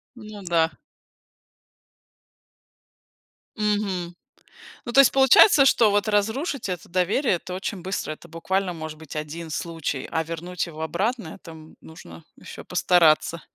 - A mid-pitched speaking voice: Yes, medium, 180 Hz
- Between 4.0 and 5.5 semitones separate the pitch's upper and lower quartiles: Yes, average, 4.5 semitones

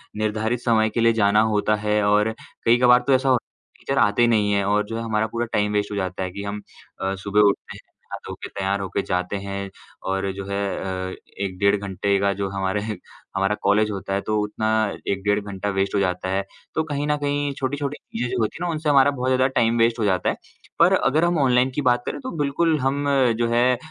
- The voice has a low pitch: Yes, low, 105 Hz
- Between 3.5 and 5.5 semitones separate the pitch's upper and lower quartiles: Yes, average, 3.9 semitones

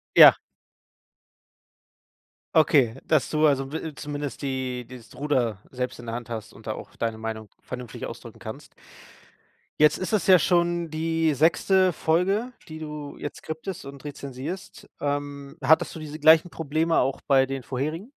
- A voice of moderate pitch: Yes, medium, 145 Hz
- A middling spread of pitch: Yes, average, 3.7 semitones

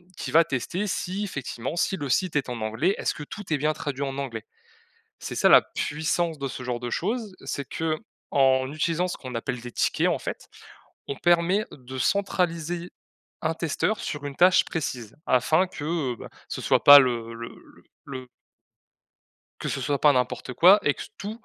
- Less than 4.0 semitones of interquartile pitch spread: No, average, 5.1 semitones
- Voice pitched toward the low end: No, medium, 150 Hz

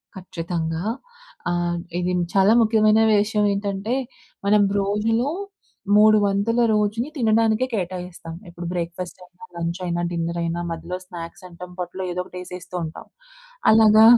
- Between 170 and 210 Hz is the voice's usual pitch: Yes, medium, 185 Hz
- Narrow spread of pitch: No, average, 3.6 semitones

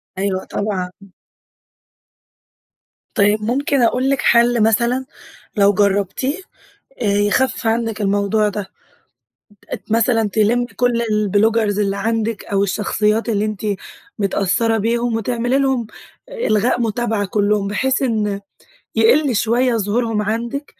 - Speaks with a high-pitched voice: Yes, high, 220 Hz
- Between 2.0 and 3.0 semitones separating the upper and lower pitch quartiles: Yes, average, 2.7 semitones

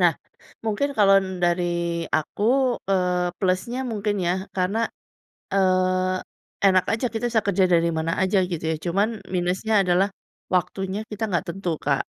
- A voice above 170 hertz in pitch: Yes, medium, 185 Hz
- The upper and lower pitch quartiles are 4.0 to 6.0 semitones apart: No, narrow, 2.4 semitones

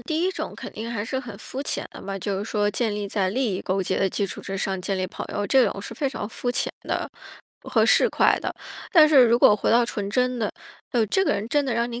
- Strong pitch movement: No, average, 4.0 semitones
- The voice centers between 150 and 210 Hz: No, high, 220 Hz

